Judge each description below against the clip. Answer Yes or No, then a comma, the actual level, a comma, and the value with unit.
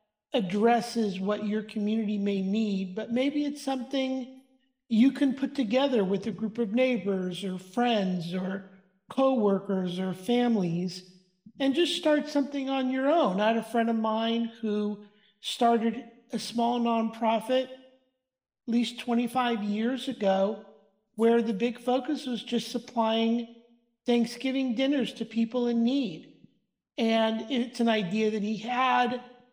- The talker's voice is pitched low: No, high, 235 Hz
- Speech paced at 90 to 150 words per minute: Yes, average, 140 wpm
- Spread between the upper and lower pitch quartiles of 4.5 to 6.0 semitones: No, average, 3.2 semitones